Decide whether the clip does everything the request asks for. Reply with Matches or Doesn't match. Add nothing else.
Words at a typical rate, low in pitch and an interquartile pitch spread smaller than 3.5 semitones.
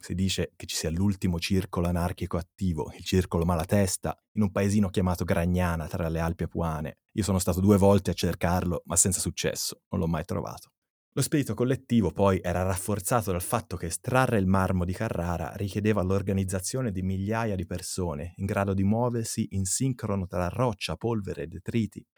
Doesn't match